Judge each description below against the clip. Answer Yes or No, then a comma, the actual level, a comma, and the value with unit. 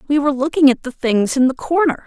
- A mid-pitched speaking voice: No, very high, 280 Hz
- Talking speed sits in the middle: No, fast, 260 wpm